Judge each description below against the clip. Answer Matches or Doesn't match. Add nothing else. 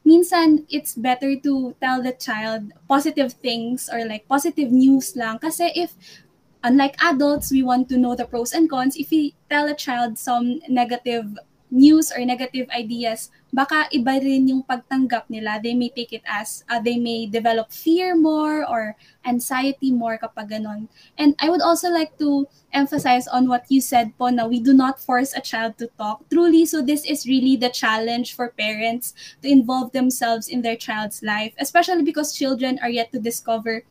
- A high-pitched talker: Matches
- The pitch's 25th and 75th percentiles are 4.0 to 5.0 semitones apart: Doesn't match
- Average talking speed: Doesn't match